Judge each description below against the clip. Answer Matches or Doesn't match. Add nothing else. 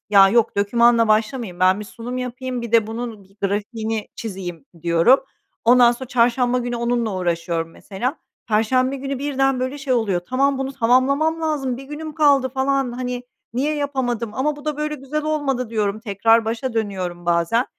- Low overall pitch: Doesn't match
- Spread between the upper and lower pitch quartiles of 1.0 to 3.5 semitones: Doesn't match